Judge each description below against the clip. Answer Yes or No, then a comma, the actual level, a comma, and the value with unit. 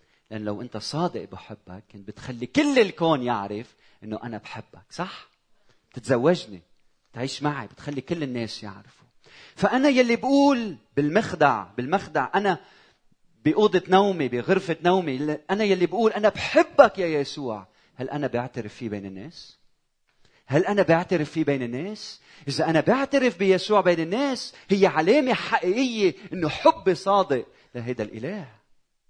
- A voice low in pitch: No, medium, 160 Hz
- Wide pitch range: Yes, wide, 8.3 semitones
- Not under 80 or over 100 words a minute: No, fast, 135 wpm